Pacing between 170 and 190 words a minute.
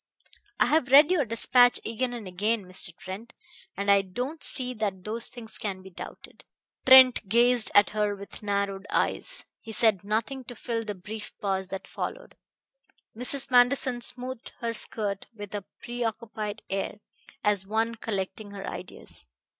No: average, 155 wpm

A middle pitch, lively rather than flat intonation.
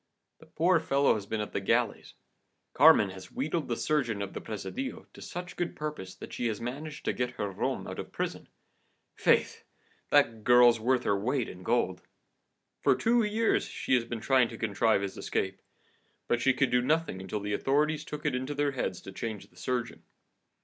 No: low, 125 Hz; wide, 5.9 semitones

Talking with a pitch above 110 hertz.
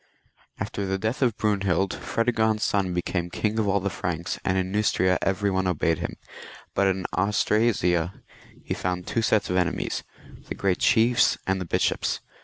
No: very low, 95 Hz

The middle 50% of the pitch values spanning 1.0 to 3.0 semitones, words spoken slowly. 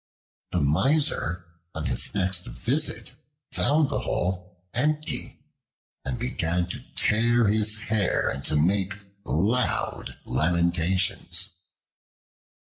No: average, 5.3 semitones; slow, 100 wpm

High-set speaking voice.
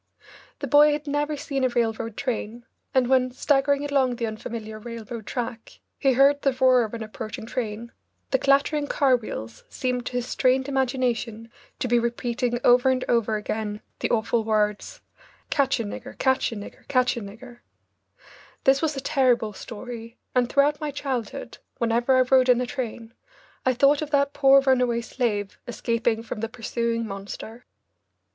Yes: high, 245 Hz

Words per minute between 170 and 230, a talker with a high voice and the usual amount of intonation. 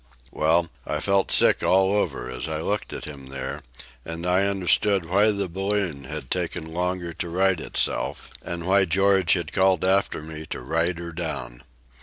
No: average, 175 wpm; very low, 85 Hz; average, 3.4 semitones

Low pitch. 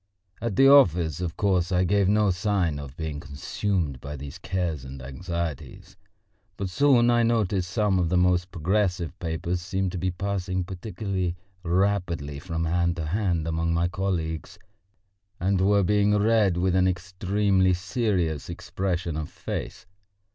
Yes: very low, 90 Hz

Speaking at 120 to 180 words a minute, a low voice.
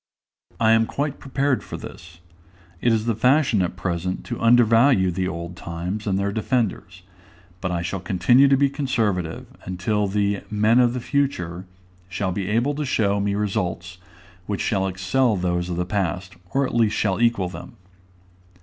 Yes: average, 170 wpm; low, 100 Hz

